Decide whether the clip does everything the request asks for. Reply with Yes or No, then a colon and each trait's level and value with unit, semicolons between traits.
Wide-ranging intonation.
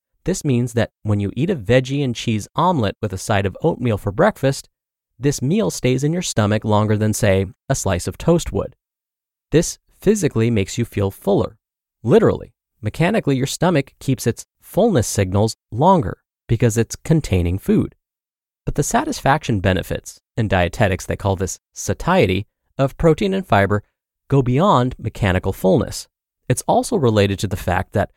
Yes: wide, 5.9 semitones